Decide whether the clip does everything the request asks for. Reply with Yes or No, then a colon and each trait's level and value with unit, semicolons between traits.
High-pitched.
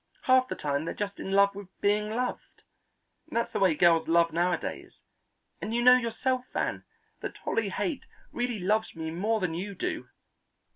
Yes: high, 205 Hz